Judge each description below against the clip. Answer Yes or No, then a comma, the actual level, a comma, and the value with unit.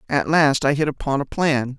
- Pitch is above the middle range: No, medium, 140 Hz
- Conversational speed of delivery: No, fast, 235 wpm